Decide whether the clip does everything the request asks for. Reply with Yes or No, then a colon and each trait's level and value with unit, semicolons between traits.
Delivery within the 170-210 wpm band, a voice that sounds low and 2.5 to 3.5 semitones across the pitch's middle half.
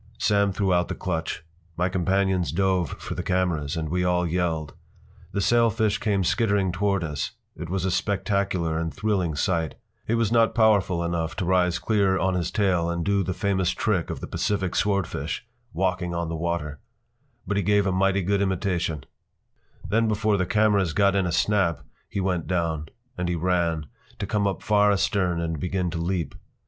Yes: average, 180 wpm; very low, 95 Hz; average, 2.8 semitones